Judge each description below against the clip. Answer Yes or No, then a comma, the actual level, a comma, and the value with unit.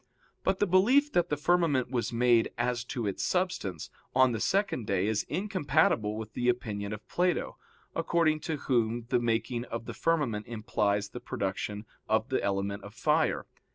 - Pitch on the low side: Yes, low, 120 Hz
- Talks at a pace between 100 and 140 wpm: No, average, 170 wpm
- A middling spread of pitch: No, wide, 6.8 semitones